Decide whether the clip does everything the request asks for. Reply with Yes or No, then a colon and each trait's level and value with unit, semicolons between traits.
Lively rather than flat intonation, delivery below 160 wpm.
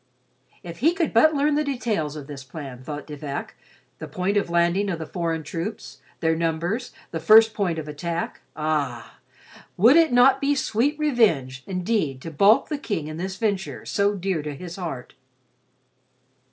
No: wide, 6.5 semitones; average, 175 wpm